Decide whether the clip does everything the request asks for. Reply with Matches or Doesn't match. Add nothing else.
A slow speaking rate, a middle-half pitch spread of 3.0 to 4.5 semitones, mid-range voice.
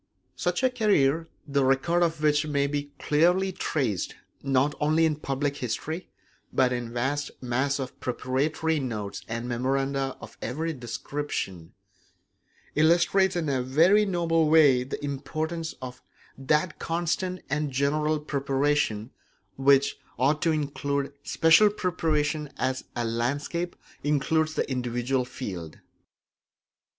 Matches